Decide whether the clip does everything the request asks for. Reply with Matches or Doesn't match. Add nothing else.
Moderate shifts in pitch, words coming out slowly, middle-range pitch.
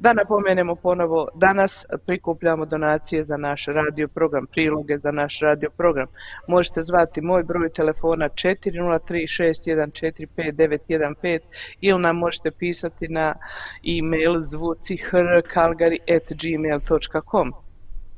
Doesn't match